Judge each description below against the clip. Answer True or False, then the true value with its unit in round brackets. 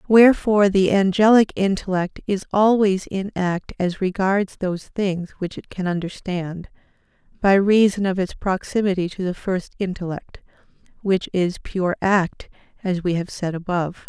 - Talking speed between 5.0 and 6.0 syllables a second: False (4.6 syllables/s)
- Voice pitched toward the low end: False (190 Hz)